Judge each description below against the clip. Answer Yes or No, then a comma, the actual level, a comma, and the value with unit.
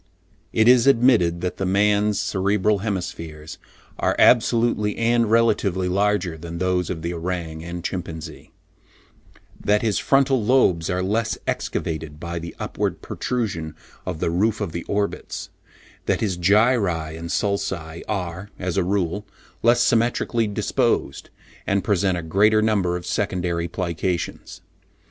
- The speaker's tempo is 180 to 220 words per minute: No, slow, 135 wpm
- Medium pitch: No, very low, 95 Hz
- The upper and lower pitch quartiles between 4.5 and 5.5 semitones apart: No, average, 3.8 semitones